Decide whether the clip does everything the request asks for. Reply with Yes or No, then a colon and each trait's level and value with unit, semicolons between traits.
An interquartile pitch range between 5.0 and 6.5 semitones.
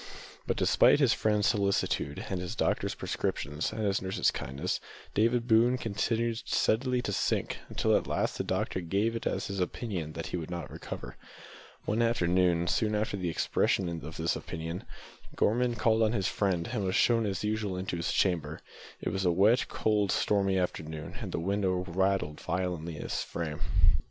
No: average, 4.2 semitones